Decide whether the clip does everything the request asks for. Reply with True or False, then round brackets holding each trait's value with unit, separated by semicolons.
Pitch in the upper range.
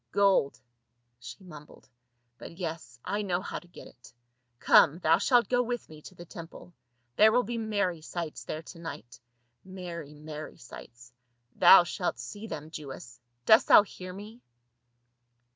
False (170 Hz)